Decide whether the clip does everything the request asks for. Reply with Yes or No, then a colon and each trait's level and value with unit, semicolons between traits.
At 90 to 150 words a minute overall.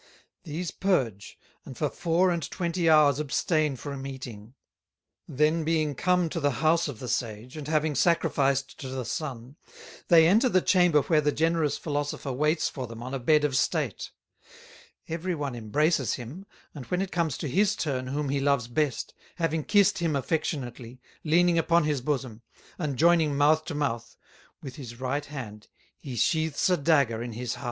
No: average, 175 wpm